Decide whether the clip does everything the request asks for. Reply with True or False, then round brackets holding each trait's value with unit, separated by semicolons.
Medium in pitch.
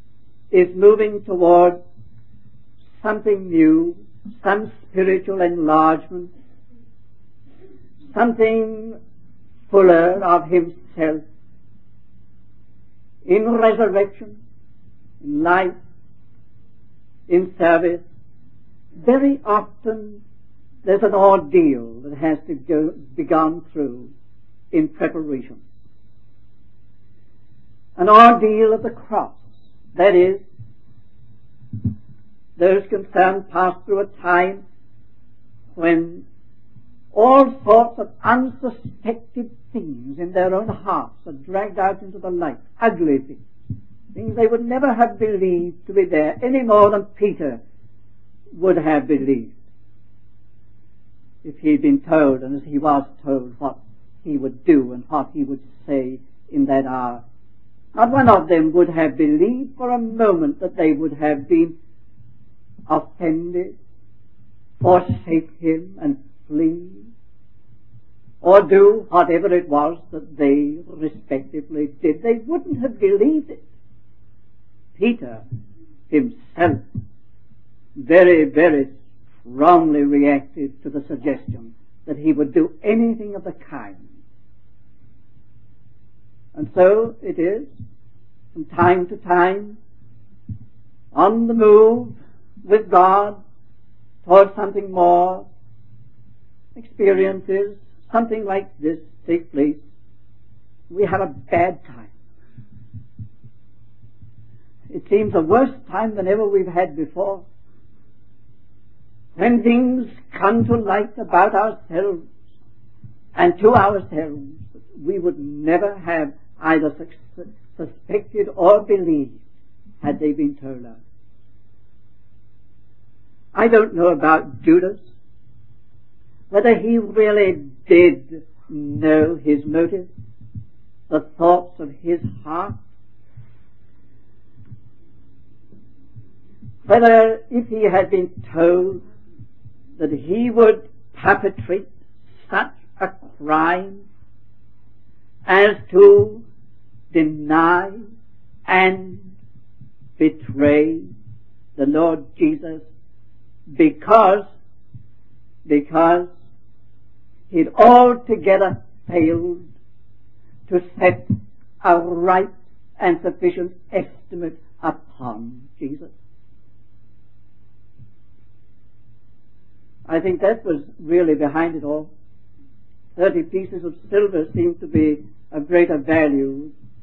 True (145 Hz)